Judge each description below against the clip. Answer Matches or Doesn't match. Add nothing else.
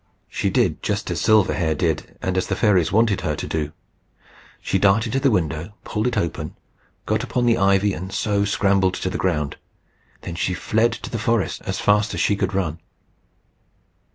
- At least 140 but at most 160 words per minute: Doesn't match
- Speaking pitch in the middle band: Doesn't match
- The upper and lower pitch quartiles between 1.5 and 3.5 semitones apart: Matches